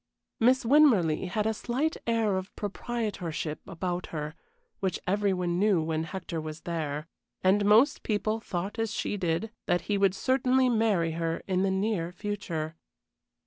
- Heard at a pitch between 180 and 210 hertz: Yes, high, 190 Hz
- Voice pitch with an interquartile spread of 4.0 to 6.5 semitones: Yes, average, 4.6 semitones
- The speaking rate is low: No, average, 155 wpm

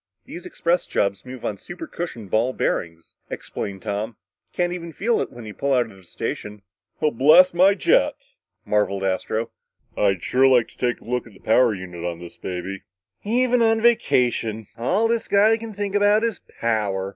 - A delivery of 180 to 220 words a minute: Yes, average, 185 wpm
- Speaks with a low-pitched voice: Yes, low, 125 Hz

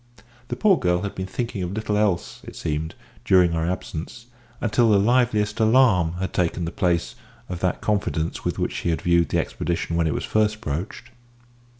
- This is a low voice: Yes, very low, 95 Hz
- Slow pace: No, average, 190 wpm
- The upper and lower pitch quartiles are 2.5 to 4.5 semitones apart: Yes, average, 4.2 semitones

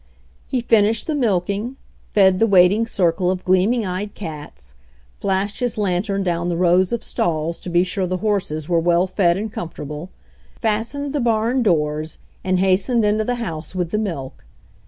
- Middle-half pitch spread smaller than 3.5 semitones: No, average, 4.0 semitones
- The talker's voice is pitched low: No, high, 190 Hz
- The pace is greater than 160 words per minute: Yes, average, 170 wpm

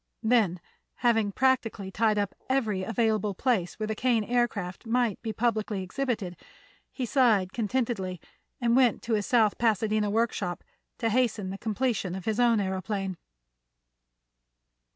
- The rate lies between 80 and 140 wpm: Yes, slow, 135 wpm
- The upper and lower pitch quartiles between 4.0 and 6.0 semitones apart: No, average, 3.4 semitones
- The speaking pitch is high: Yes, high, 220 Hz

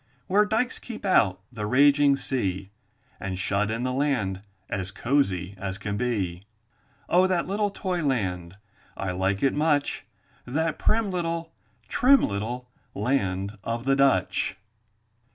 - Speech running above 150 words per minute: No, slow, 135 wpm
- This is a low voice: Yes, low, 125 Hz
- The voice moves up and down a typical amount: No, wide, 8.5 semitones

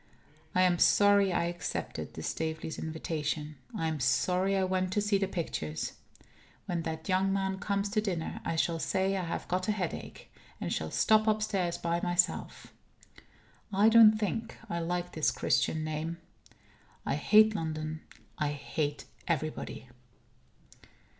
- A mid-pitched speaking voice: Yes, medium, 175 Hz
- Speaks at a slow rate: No, average, 145 wpm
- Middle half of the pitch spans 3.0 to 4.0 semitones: Yes, average, 3.6 semitones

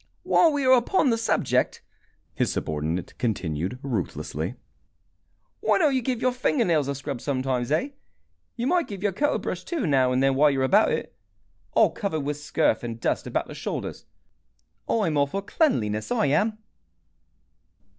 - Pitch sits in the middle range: Yes, medium, 150 Hz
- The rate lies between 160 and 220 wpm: Yes, average, 170 wpm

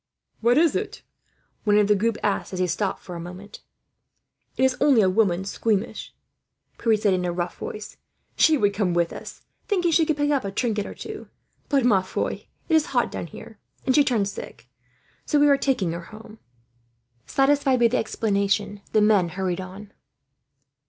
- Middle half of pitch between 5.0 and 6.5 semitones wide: Yes, wide, 5.4 semitones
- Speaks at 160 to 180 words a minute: No, average, 190 wpm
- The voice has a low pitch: No, high, 210 Hz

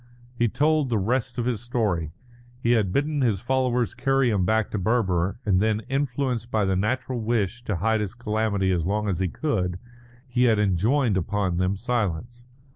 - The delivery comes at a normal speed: Yes, average, 185 wpm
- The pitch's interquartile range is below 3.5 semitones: No, average, 4.2 semitones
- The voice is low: Yes, low, 110 Hz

